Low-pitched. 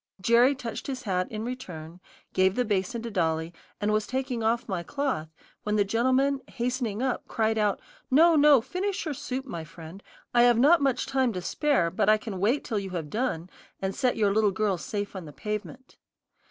No: high, 220 Hz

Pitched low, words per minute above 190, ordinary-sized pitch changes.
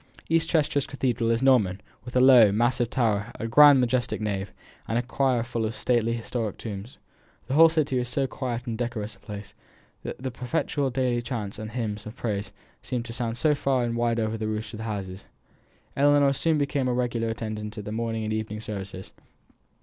Yes: low, 120 Hz; average, 200 wpm; average, 3.0 semitones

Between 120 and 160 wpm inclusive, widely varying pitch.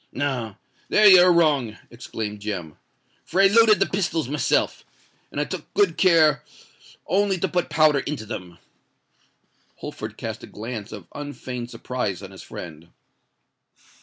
Yes: average, 140 wpm; wide, 8.7 semitones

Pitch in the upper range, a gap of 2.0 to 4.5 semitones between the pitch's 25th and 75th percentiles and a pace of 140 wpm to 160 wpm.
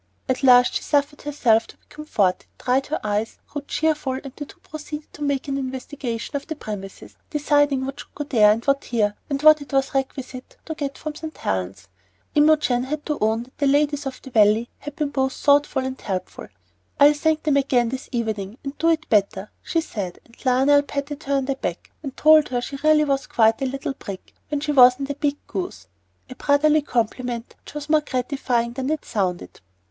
No: very high, 275 Hz; average, 3.4 semitones; fast, 205 wpm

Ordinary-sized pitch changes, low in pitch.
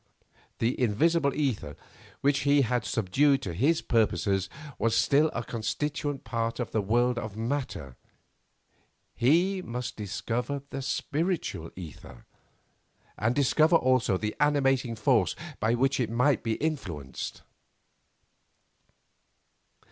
Yes: average, 4.5 semitones; low, 120 Hz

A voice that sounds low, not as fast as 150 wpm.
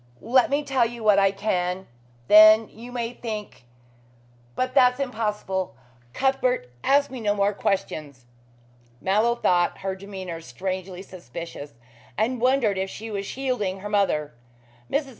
No: high, 210 Hz; average, 140 wpm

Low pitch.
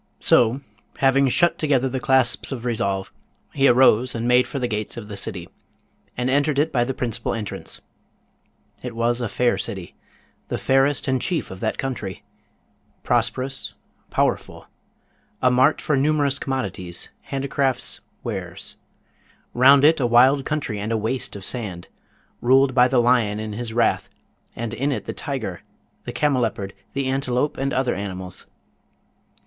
Yes: low, 125 Hz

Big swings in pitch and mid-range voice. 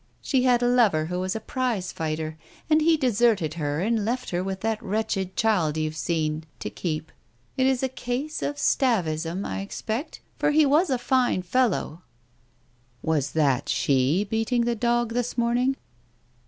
No: wide, 7.4 semitones; high, 220 Hz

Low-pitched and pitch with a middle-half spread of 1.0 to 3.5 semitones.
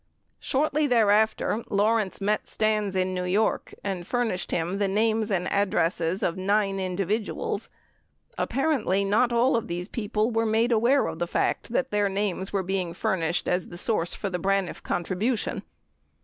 No: high, 200 Hz; average, 3.1 semitones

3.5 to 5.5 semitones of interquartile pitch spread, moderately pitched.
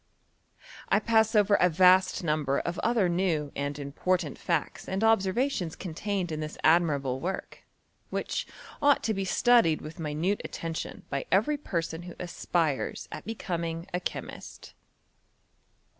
Yes: average, 4.2 semitones; medium, 175 Hz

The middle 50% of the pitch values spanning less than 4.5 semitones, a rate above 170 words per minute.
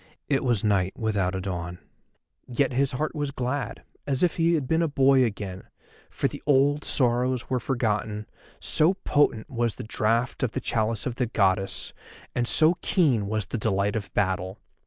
No: average, 4.8 semitones; average, 180 wpm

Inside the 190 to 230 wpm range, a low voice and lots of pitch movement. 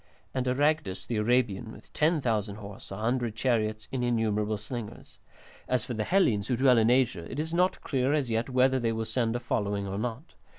No: average, 200 wpm; low, 120 Hz; average, 3.2 semitones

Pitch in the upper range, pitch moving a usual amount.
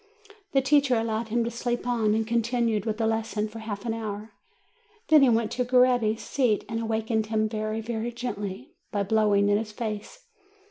No: high, 225 Hz; narrow, 1.9 semitones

